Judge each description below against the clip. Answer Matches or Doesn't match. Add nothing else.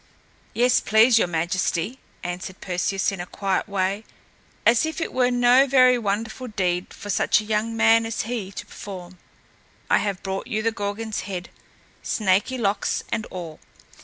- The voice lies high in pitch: Matches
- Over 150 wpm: Matches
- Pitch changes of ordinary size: Matches